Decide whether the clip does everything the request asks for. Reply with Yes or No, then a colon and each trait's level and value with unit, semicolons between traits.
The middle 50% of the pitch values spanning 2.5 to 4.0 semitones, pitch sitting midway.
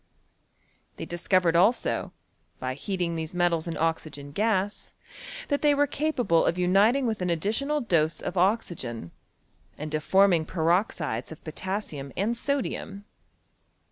No: average, 5.1 semitones; medium, 180 Hz